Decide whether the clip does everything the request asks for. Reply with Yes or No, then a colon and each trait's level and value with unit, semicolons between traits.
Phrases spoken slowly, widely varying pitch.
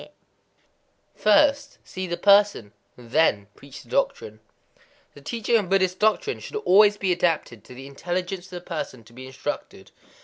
No: average, 160 wpm; wide, 7.3 semitones